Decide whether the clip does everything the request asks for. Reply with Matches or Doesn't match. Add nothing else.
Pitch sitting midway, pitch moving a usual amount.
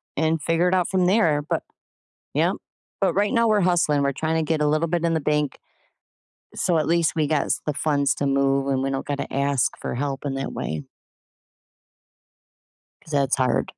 Matches